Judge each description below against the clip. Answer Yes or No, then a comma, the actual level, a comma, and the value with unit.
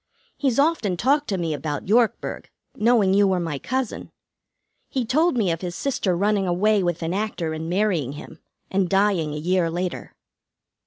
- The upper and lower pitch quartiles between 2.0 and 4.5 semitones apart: Yes, average, 4.2 semitones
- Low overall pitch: No, high, 190 Hz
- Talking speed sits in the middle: Yes, average, 170 wpm